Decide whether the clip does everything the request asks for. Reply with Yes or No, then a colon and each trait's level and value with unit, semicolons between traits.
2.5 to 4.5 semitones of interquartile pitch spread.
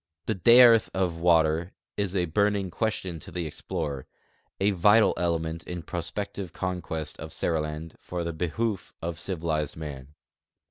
Yes: average, 3.3 semitones